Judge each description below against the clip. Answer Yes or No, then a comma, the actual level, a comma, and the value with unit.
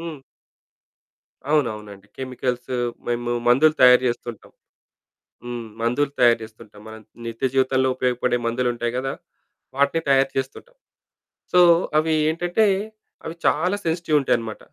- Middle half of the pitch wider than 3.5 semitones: Yes, average, 3.9 semitones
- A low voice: Yes, low, 125 Hz